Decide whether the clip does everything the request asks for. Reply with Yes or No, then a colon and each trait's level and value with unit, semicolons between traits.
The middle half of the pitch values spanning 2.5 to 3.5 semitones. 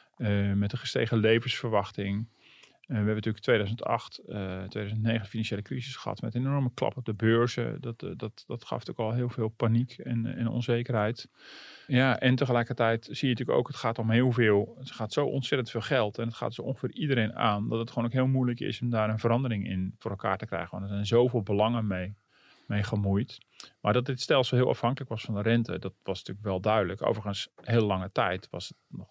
Yes: average, 2.9 semitones